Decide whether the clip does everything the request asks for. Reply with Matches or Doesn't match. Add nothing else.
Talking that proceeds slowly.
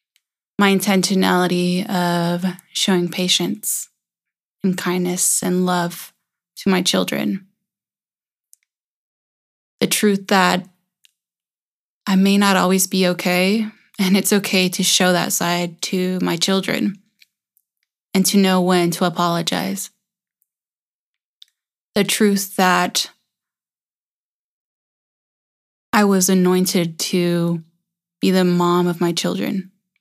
Matches